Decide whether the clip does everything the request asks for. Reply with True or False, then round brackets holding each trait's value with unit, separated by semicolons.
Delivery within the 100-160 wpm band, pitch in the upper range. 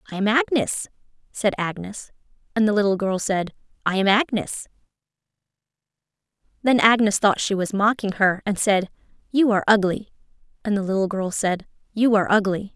True (155 wpm; 205 Hz)